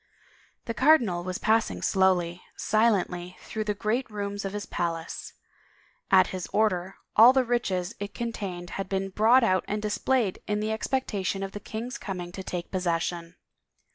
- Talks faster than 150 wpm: Yes, average, 160 wpm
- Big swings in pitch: No, average, 3.2 semitones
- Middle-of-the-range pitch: No, high, 200 Hz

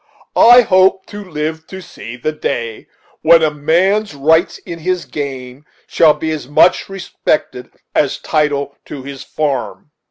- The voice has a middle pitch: Yes, medium, 155 Hz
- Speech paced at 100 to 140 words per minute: No, average, 155 wpm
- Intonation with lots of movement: No, average, 4.5 semitones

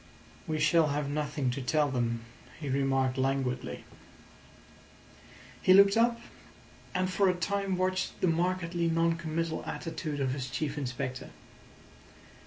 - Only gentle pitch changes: No, average, 4.8 semitones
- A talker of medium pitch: Yes, medium, 155 Hz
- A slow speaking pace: Yes, slow, 130 wpm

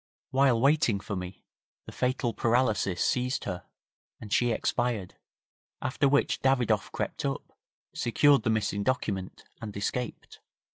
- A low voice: Yes, low, 115 Hz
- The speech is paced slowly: Yes, slow, 130 wpm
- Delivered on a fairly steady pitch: No, average, 4.2 semitones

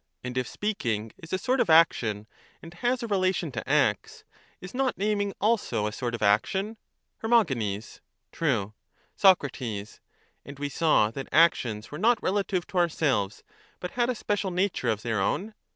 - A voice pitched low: No, medium, 165 Hz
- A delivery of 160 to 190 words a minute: Yes, average, 170 wpm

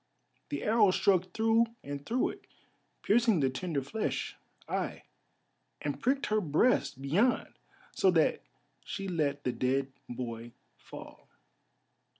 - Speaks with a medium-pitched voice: Yes, medium, 175 Hz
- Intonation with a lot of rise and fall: Yes, wide, 8.3 semitones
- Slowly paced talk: Yes, slow, 125 wpm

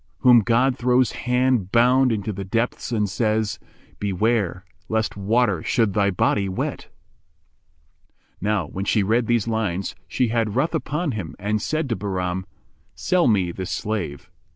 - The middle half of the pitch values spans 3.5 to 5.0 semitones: Yes, average, 3.8 semitones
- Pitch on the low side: Yes, low, 110 Hz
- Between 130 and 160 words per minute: Yes, average, 155 wpm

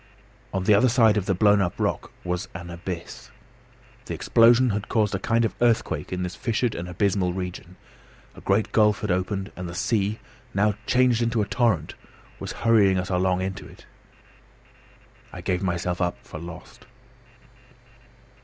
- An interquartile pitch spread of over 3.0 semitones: Yes, average, 3.5 semitones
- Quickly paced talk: No, average, 165 wpm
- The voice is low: Yes, very low, 95 Hz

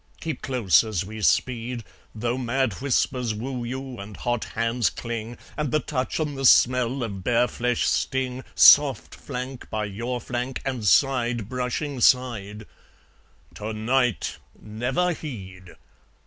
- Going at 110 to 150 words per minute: Yes, slow, 135 wpm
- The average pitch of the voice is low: Yes, low, 120 Hz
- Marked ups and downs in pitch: No, average, 2.9 semitones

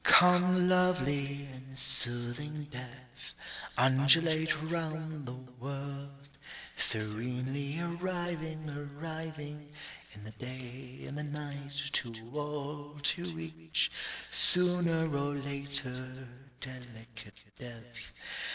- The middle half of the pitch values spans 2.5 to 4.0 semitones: Yes, average, 3.7 semitones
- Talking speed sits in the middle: No, slow, 85 wpm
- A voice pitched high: No, medium, 140 Hz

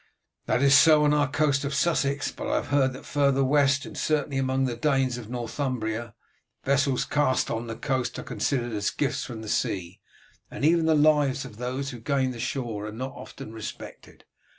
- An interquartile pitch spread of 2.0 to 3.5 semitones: Yes, average, 2.9 semitones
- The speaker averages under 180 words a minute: No, average, 200 wpm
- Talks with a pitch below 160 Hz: Yes, low, 135 Hz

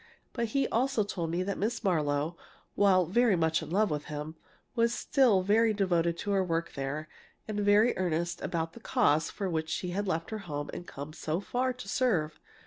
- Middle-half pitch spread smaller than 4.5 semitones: No, average, 5.0 semitones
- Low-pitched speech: No, medium, 185 Hz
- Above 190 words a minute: Yes, average, 200 wpm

